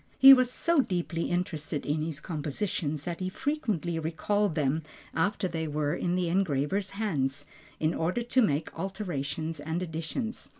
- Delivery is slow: No, average, 155 wpm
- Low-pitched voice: No, medium, 170 Hz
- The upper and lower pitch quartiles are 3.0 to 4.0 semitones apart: No, average, 4.5 semitones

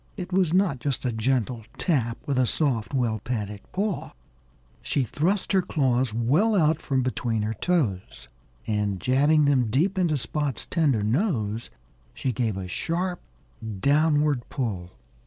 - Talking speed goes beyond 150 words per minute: No, average, 145 wpm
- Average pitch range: No, wide, 5.9 semitones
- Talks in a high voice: No, low, 130 Hz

